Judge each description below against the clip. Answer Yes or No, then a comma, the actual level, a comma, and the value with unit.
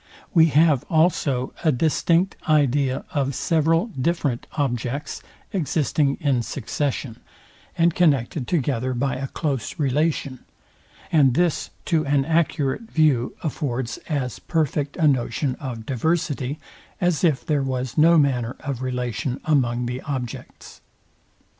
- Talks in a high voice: No, medium, 140 Hz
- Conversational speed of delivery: No, slow, 120 wpm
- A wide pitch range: No, average, 3.8 semitones